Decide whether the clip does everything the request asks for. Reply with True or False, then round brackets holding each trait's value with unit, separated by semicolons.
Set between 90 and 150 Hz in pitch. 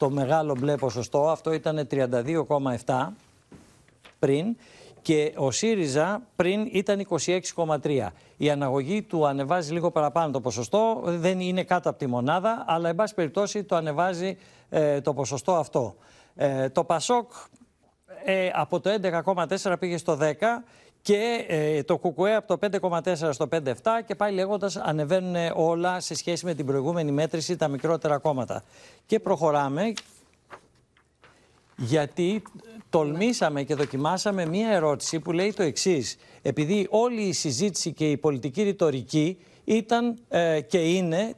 False (170 Hz)